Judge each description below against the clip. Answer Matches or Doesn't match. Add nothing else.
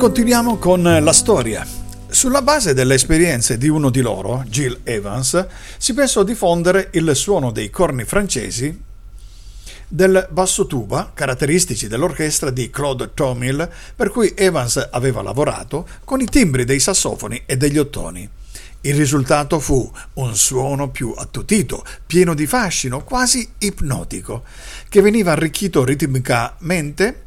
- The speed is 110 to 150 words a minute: Matches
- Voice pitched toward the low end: Doesn't match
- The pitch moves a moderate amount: Doesn't match